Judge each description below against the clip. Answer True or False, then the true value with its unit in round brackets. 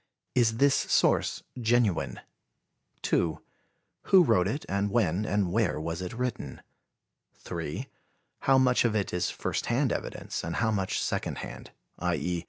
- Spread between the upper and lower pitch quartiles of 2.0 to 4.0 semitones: False (5.2 semitones)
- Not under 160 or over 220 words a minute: False (150 wpm)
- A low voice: True (105 Hz)